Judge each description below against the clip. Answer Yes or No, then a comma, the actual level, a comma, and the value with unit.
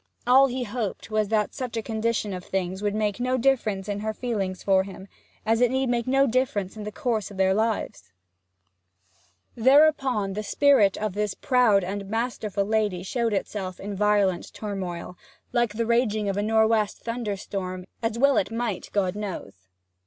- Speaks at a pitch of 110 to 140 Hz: No, high, 215 Hz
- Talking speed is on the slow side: No, average, 175 wpm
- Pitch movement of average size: Yes, average, 3.3 semitones